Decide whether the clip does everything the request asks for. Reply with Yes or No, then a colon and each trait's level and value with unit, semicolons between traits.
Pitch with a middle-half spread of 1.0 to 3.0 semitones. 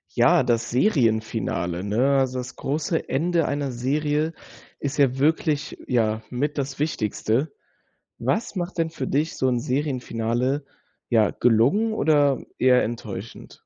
No: average, 4.1 semitones